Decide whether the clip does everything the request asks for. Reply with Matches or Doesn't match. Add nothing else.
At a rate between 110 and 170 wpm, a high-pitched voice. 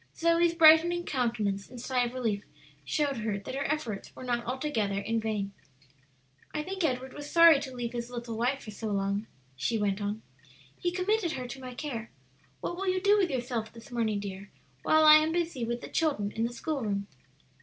Doesn't match